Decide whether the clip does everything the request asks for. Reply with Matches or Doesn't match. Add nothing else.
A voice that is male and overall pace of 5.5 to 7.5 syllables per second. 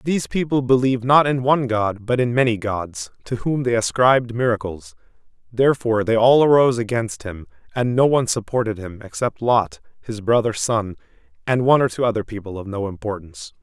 Matches